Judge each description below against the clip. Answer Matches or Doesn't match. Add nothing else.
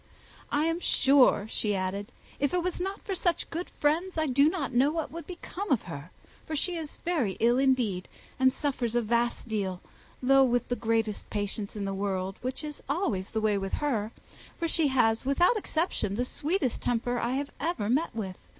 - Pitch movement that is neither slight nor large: Doesn't match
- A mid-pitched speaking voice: Doesn't match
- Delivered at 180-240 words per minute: Matches